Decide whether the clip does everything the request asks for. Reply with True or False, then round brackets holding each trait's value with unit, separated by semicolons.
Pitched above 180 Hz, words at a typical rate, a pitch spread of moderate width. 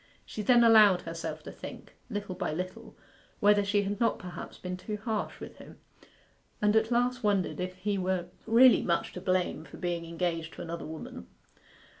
True (190 Hz; 180 wpm; 3.3 semitones)